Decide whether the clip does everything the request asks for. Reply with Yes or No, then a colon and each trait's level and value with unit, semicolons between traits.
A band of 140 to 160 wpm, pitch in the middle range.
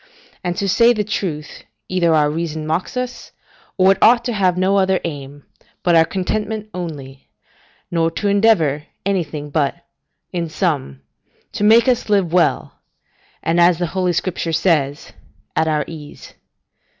Yes: average, 150 wpm; medium, 175 Hz